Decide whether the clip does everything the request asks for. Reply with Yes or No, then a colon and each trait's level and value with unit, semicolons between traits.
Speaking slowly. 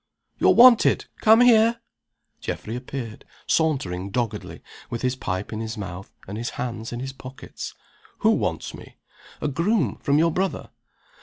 No: average, 150 wpm